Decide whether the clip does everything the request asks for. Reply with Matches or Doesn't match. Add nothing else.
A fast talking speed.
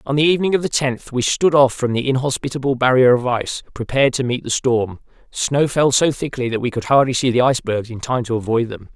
Matches